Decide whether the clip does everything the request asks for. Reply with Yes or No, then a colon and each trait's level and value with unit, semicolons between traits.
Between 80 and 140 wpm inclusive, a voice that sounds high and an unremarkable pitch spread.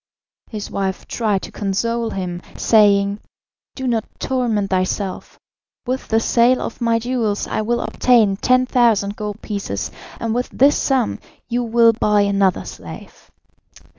Yes: slow, 135 wpm; high, 220 Hz; average, 3.0 semitones